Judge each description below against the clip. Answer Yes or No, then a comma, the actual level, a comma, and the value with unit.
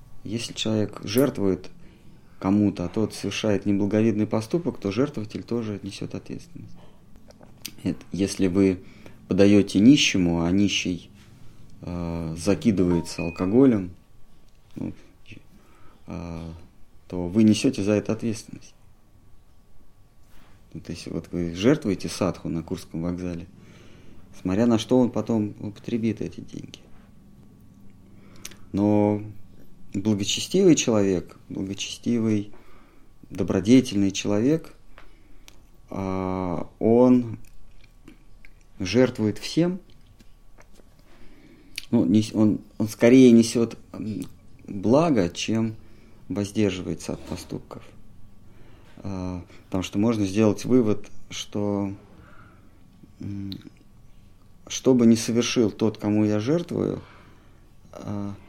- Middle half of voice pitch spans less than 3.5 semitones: Yes, average, 2.8 semitones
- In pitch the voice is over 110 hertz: No, low, 100 Hz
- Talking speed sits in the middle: No, slow, 85 wpm